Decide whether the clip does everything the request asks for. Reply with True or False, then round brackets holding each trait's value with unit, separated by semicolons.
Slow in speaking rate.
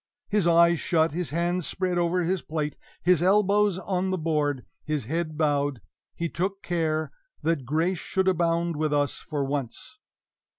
False (160 wpm)